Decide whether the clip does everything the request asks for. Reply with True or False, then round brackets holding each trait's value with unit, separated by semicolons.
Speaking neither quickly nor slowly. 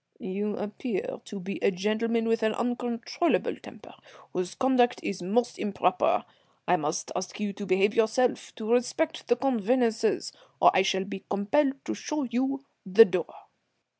True (155 wpm)